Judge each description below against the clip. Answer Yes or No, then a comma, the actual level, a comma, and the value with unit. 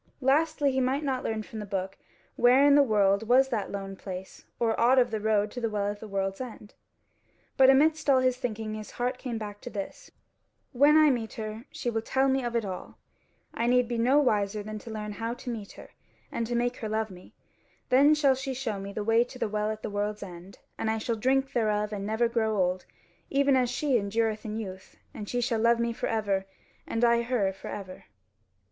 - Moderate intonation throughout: Yes, average, 3.4 semitones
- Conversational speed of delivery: No, fast, 230 wpm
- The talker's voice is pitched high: Yes, high, 225 Hz